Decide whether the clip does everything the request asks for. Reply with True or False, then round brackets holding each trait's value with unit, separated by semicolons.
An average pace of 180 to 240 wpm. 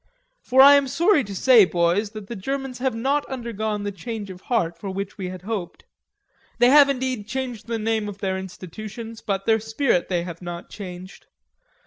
True (190 wpm)